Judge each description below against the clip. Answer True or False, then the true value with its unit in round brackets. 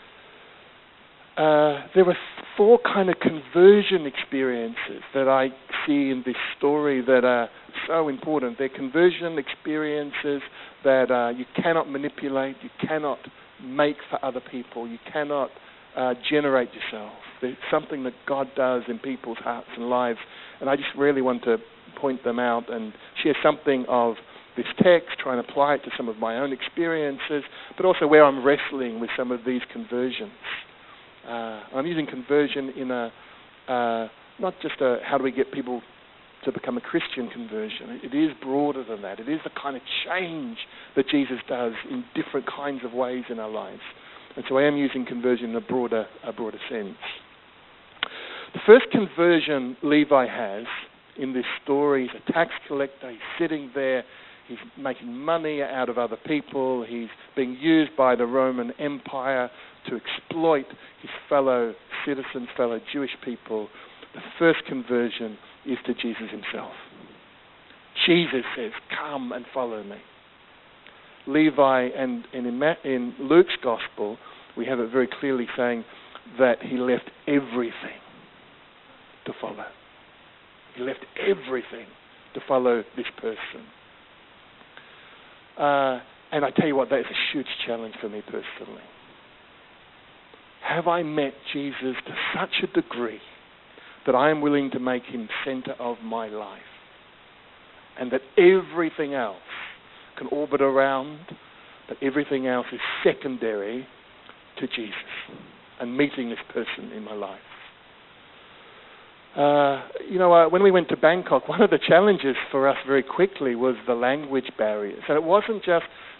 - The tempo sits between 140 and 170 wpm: True (150 wpm)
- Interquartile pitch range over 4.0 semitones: False (3.4 semitones)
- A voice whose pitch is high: False (135 Hz)